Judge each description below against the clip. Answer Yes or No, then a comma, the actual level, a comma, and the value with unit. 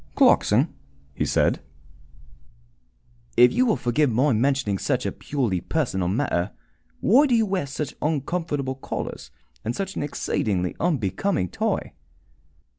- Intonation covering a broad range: Yes, wide, 7.6 semitones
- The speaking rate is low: Yes, slow, 120 wpm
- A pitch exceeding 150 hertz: No, medium, 140 Hz